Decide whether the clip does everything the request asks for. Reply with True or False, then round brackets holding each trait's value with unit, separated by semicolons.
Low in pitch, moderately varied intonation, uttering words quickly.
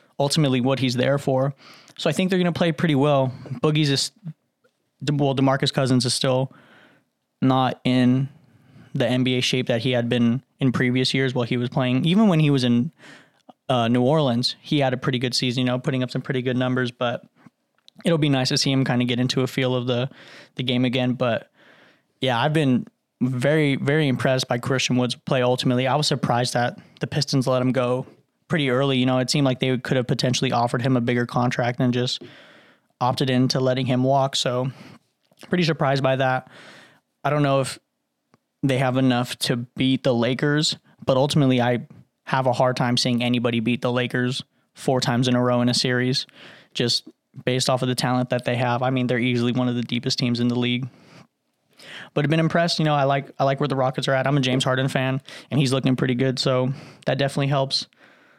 False (130 Hz; 1.8 semitones; 215 wpm)